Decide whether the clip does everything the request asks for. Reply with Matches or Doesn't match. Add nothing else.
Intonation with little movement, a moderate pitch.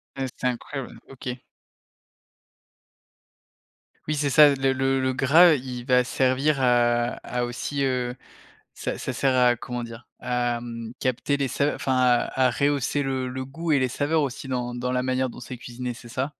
Doesn't match